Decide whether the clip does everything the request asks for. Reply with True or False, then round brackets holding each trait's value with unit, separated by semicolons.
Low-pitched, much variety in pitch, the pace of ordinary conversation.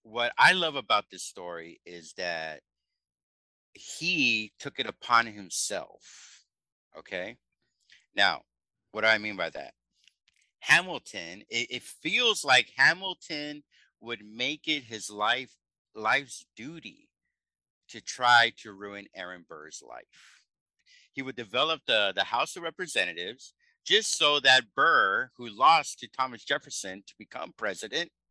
False (115 Hz; 5.9 semitones; 130 wpm)